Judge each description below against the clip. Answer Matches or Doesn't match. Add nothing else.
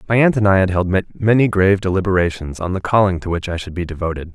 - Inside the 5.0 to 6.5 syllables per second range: Doesn't match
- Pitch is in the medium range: Doesn't match